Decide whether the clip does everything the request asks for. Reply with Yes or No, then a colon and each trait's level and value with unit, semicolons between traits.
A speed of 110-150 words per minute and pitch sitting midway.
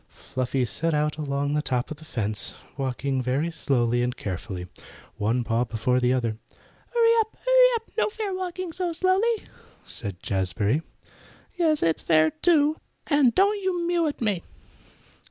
No: average, 160 wpm; medium, 150 Hz